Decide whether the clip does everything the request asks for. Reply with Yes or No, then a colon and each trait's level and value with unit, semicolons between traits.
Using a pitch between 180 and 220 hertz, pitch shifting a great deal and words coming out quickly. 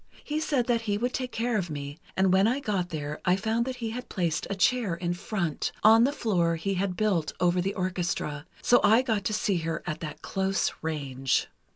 No: high, 190 Hz; average, 5.0 semitones; fast, 220 wpm